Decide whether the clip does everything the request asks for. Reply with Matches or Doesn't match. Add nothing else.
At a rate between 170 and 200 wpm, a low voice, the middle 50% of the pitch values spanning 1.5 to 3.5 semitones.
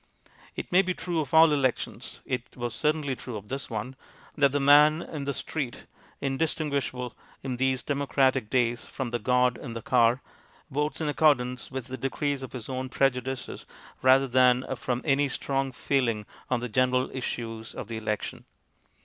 Matches